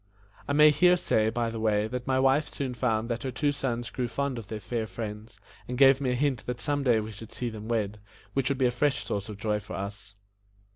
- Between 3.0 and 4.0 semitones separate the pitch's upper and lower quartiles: Yes, average, 3.6 semitones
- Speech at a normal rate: No, fast, 250 wpm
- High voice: No, low, 120 Hz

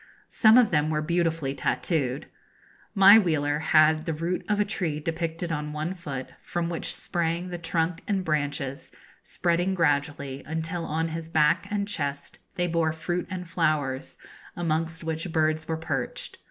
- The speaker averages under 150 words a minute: No, average, 155 wpm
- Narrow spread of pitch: Yes, narrow, 2.3 semitones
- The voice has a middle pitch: Yes, medium, 160 Hz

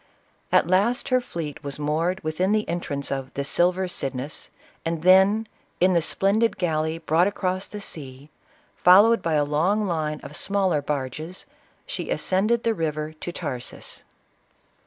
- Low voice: No, medium, 170 Hz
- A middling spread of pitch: Yes, average, 4.3 semitones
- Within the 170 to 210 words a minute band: No, average, 160 wpm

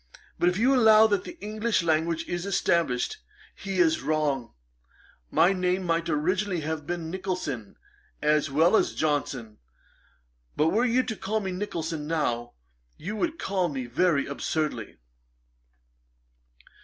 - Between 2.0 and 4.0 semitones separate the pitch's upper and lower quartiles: No, average, 4.8 semitones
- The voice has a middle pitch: Yes, medium, 170 Hz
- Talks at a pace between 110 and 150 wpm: Yes, slow, 135 wpm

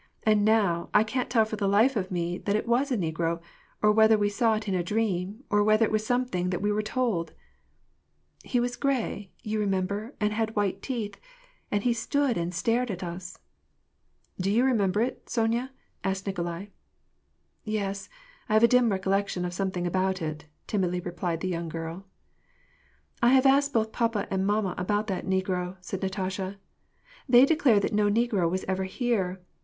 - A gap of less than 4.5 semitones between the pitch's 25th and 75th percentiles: Yes, average, 3.5 semitones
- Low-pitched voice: No, high, 205 Hz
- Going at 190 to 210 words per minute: Yes, average, 200 wpm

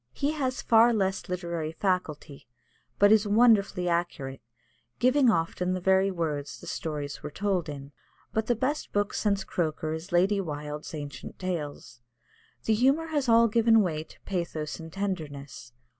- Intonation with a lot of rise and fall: Yes, wide, 5.9 semitones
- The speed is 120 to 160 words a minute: Yes, average, 155 wpm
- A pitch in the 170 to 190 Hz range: Yes, medium, 185 Hz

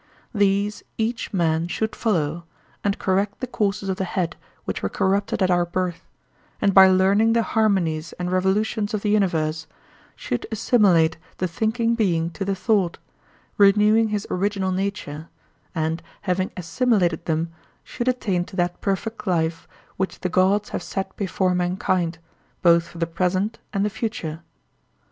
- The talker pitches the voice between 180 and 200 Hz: Yes, high, 190 Hz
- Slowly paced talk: No, average, 155 wpm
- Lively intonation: No, average, 3.2 semitones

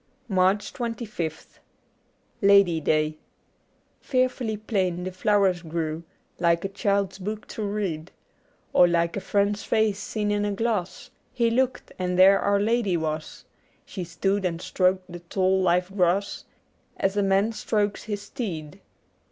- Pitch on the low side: No, high, 195 Hz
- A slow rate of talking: No, average, 145 wpm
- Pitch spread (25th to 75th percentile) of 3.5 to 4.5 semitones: No, average, 2.9 semitones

